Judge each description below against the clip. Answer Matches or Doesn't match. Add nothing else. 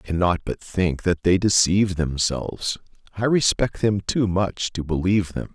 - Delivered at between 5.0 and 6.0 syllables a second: Doesn't match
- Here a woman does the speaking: Doesn't match